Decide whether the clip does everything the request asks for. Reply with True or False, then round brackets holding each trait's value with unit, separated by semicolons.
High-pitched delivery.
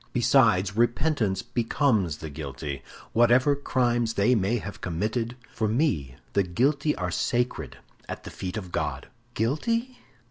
False (115 Hz)